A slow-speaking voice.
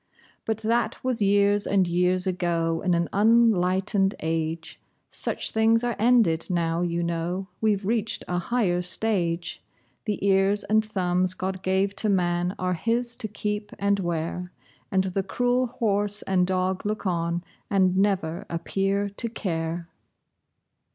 No: average, 145 wpm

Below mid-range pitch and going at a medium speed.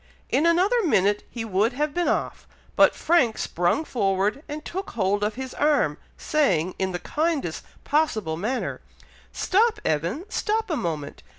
No: very high, 250 Hz; average, 155 wpm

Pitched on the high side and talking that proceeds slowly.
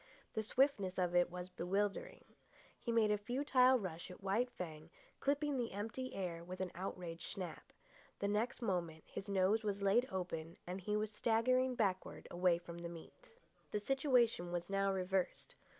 No: high, 195 Hz; average, 165 wpm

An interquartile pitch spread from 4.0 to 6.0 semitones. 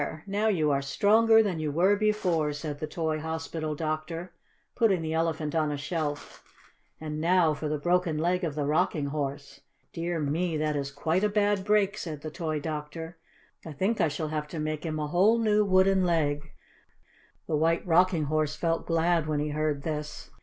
No: average, 3.0 semitones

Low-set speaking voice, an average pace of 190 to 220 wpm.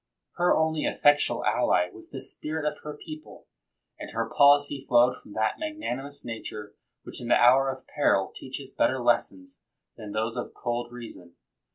No: low, 130 Hz; average, 170 wpm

